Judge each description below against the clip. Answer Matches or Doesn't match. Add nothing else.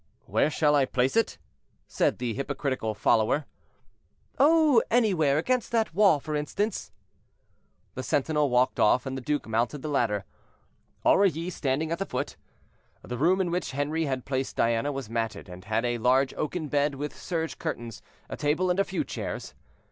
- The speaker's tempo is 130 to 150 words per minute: Doesn't match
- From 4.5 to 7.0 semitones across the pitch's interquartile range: Matches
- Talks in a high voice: Doesn't match